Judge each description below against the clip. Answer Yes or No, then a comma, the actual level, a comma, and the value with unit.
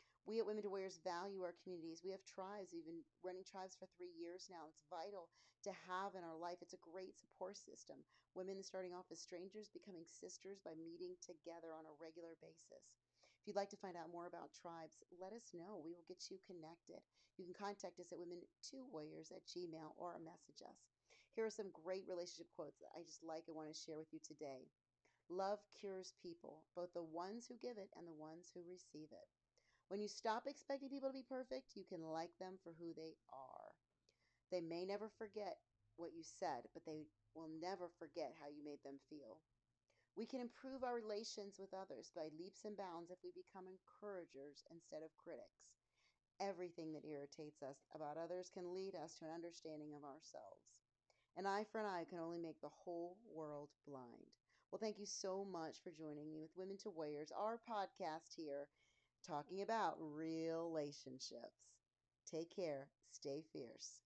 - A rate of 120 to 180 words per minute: No, average, 190 wpm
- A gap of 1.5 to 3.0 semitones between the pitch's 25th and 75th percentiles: No, average, 3.4 semitones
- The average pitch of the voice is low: No, medium, 175 Hz